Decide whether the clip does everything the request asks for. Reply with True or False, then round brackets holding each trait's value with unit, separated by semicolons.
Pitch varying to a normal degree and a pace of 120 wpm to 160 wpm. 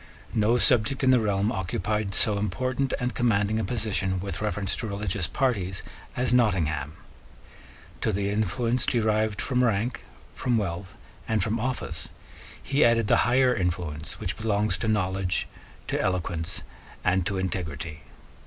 True (3.9 semitones; 145 wpm)